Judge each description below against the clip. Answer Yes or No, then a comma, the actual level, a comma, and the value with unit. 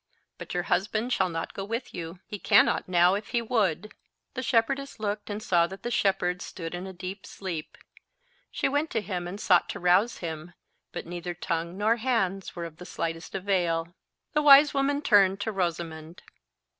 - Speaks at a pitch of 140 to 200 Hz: Yes, high, 190 Hz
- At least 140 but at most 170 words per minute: No, average, 185 wpm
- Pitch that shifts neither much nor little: Yes, average, 4.1 semitones